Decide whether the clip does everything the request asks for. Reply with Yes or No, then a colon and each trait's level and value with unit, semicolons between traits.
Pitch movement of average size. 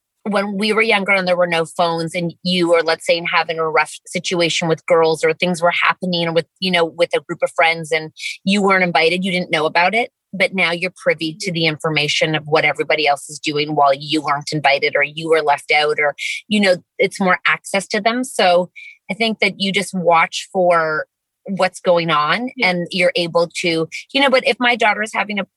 Yes: average, 3.0 semitones